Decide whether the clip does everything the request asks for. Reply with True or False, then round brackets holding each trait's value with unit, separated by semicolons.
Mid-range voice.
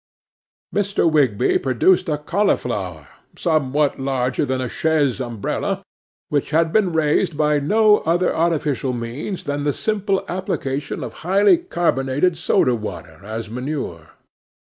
True (150 Hz)